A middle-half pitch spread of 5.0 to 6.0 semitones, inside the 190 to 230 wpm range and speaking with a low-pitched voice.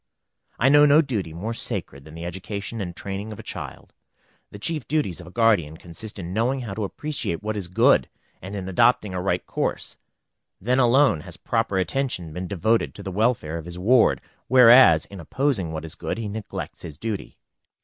Yes: average, 5.3 semitones; average, 195 wpm; low, 100 Hz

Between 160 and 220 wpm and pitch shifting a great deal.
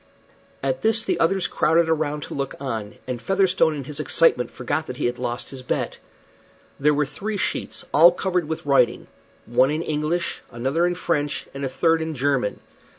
No: average, 185 wpm; average, 4.1 semitones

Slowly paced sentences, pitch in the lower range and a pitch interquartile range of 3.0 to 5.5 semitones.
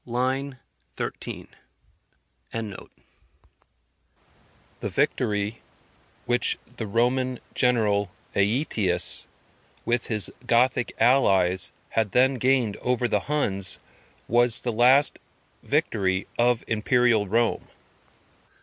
Yes: slow, 85 wpm; low, 115 Hz; average, 3.4 semitones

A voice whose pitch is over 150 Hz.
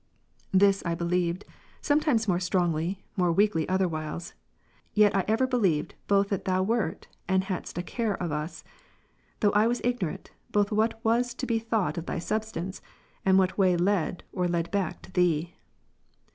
Yes: high, 190 Hz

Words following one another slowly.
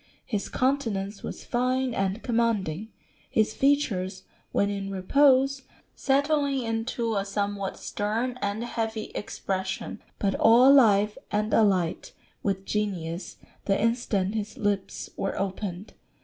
Yes: slow, 120 wpm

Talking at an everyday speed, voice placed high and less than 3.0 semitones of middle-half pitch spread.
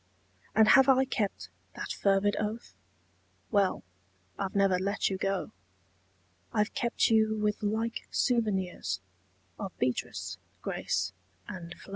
No: slow, 120 wpm; high, 205 Hz; narrow, 2.6 semitones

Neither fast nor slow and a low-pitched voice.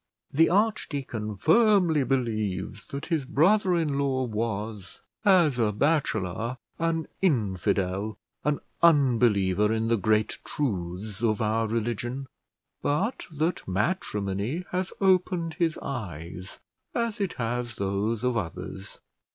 No: slow, 115 wpm; low, 120 Hz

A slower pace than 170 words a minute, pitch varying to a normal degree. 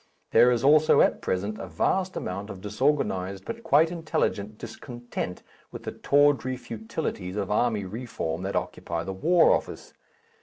No: average, 150 wpm; wide, 6.8 semitones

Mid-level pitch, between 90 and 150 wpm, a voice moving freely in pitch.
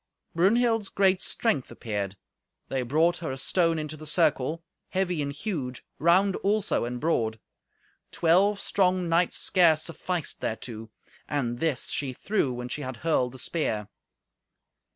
Yes: medium, 160 Hz; average, 140 wpm; wide, 6.2 semitones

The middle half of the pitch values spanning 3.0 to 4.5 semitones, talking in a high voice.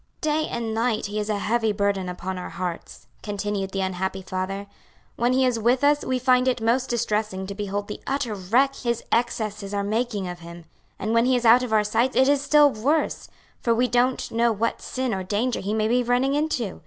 Yes: average, 3.8 semitones; high, 225 Hz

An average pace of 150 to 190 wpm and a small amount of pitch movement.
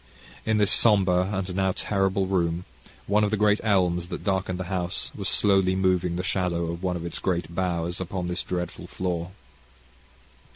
Yes: average, 175 wpm; narrow, 1.7 semitones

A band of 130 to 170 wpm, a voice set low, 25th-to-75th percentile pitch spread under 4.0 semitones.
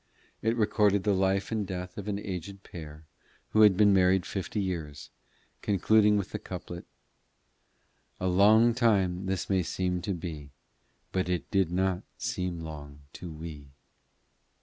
Yes: average, 150 wpm; very low, 95 Hz; average, 2.7 semitones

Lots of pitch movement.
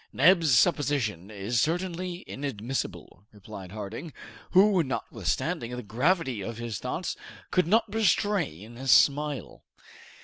Yes: wide, 8.1 semitones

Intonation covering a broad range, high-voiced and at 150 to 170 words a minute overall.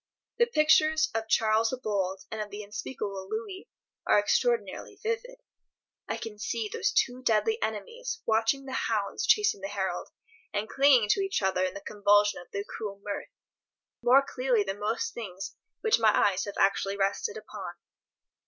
Yes: wide, 7.3 semitones; high, 220 Hz; average, 165 wpm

